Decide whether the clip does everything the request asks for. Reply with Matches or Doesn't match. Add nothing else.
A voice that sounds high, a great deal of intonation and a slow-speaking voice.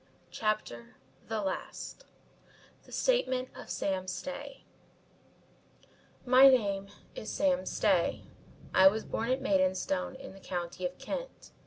Matches